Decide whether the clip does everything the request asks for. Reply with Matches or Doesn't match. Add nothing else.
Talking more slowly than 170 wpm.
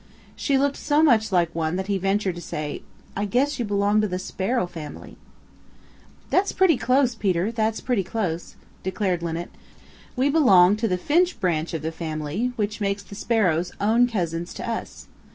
Doesn't match